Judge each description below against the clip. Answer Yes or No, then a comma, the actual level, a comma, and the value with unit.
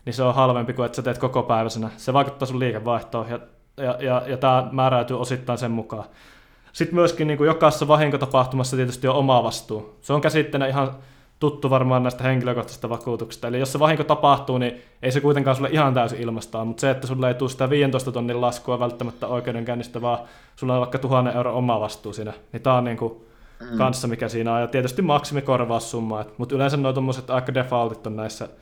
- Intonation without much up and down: Yes, narrow, 2.2 semitones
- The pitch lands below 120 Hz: No, low, 125 Hz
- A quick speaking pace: Yes, fast, 195 wpm